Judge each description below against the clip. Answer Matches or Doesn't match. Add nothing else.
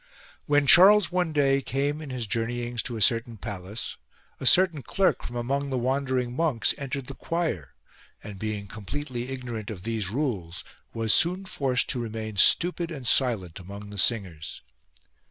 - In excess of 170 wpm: Doesn't match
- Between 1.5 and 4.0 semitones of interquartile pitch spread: Doesn't match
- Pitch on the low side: Matches